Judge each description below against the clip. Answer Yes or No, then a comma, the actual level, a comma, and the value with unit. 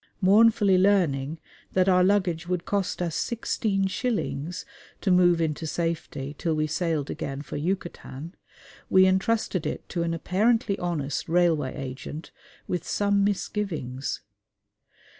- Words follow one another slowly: Yes, slow, 125 wpm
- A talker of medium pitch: Yes, medium, 175 Hz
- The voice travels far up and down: No, average, 3.9 semitones